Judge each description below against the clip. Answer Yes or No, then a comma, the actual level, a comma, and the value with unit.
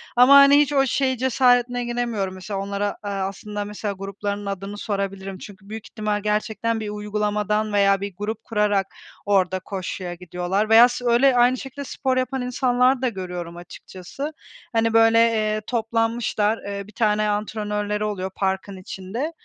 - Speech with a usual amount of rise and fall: Yes, average, 3.3 semitones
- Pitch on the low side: No, high, 210 Hz